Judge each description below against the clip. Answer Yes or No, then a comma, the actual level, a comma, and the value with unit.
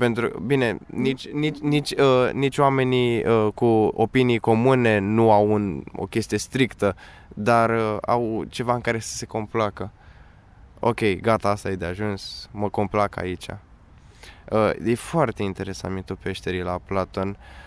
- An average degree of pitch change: Yes, average, 3.8 semitones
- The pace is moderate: Yes, average, 145 wpm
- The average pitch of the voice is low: Yes, low, 110 Hz